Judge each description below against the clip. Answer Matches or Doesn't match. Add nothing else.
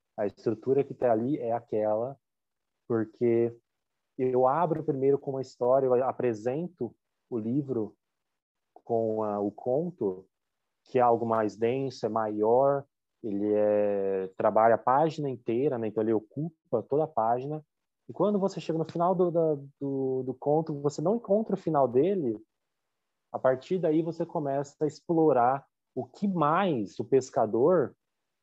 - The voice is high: Doesn't match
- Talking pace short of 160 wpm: Matches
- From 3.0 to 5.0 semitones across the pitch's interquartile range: Doesn't match